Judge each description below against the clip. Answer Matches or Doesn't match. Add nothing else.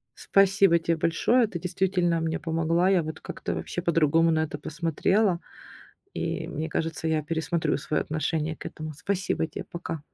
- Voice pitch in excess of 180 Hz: Doesn't match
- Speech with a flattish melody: Matches